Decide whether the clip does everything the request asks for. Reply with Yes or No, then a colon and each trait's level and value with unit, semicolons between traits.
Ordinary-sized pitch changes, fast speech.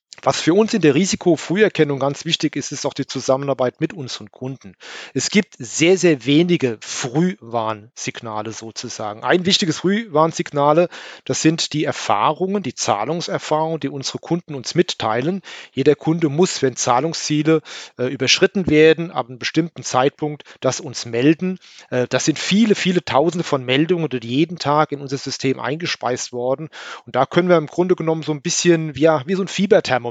No: average, 4.6 semitones; average, 165 wpm